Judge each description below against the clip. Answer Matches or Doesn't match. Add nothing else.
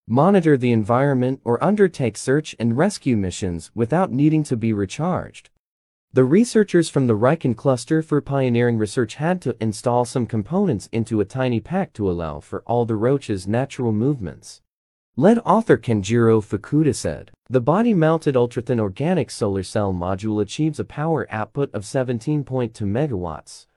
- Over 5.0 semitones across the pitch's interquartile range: Matches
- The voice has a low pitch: Matches